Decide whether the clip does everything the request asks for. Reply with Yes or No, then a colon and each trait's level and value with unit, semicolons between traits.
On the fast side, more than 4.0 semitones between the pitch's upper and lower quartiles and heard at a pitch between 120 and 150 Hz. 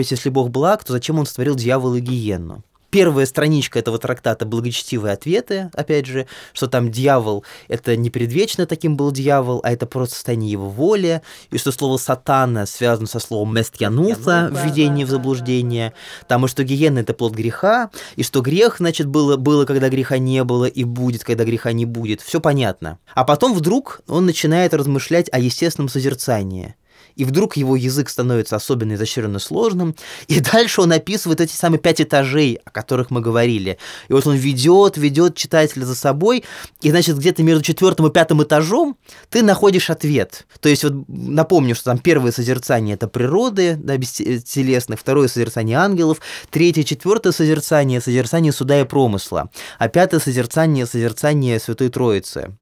Yes: fast, 165 wpm; average, 4.9 semitones; low, 135 Hz